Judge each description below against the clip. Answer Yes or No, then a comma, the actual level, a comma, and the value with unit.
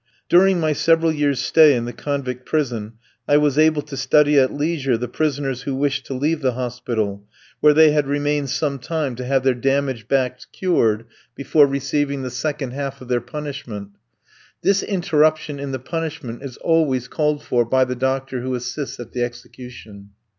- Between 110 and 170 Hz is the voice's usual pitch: Yes, low, 135 Hz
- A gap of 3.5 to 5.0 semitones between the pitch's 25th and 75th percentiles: No, average, 3.0 semitones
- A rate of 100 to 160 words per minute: No, average, 180 wpm